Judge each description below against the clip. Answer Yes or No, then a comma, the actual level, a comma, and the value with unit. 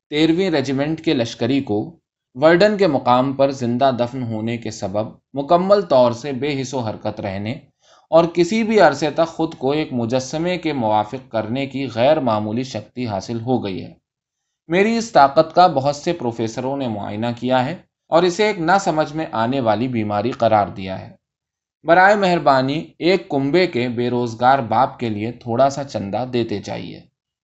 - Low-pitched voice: Yes, low, 130 Hz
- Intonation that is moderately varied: No, wide, 5.7 semitones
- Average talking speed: Yes, average, 175 wpm